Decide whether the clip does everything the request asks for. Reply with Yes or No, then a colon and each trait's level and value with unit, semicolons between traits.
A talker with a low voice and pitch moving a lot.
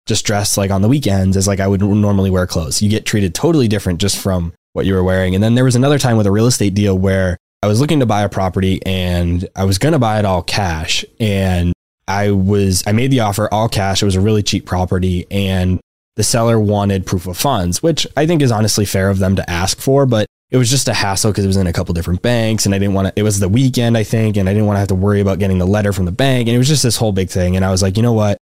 No: low, 100 Hz; average, 2.7 semitones